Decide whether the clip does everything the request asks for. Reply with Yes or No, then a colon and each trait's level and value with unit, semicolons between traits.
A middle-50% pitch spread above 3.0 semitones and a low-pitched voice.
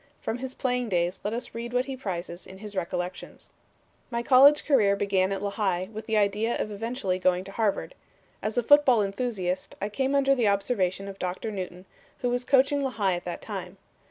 No: average, 4.7 semitones; high, 210 Hz